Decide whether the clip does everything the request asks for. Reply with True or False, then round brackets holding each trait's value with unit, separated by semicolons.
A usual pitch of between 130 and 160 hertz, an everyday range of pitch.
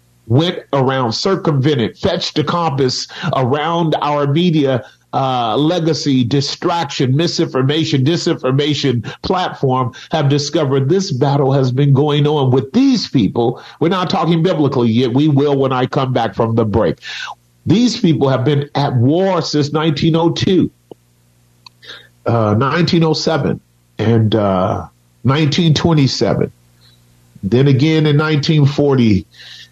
True (140 Hz; 5.0 semitones)